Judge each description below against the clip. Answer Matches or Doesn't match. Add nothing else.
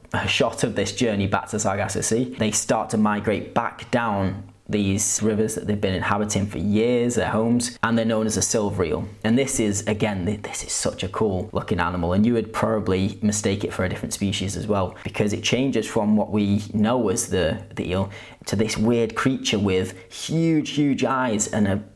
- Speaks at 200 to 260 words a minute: Matches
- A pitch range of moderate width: Doesn't match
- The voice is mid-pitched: Doesn't match